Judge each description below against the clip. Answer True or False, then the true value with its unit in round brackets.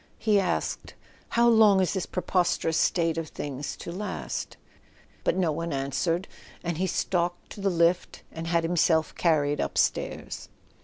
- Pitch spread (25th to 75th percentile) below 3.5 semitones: True (2.6 semitones)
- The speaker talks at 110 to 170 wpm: True (155 wpm)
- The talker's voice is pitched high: False (170 Hz)